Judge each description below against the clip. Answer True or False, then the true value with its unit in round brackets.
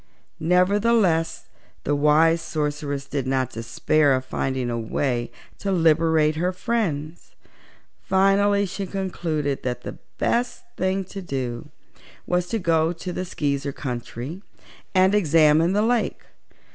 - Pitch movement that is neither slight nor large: True (4.9 semitones)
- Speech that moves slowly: True (125 wpm)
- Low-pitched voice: False (160 Hz)